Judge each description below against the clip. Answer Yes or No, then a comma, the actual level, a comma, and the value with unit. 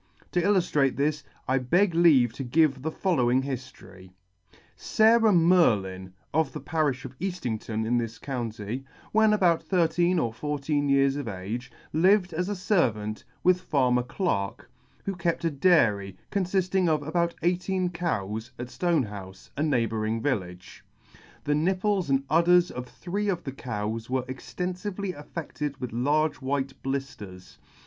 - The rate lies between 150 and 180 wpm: No, average, 140 wpm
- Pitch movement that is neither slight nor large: No, wide, 6.5 semitones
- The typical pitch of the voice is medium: Yes, medium, 145 Hz